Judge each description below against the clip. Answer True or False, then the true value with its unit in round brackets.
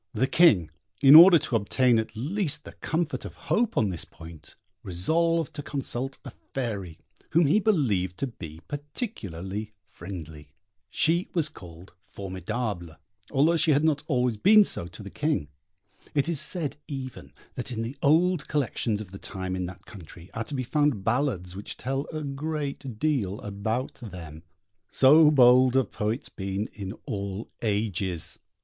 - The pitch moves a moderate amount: False (7.4 semitones)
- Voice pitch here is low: True (120 Hz)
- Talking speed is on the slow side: False (160 wpm)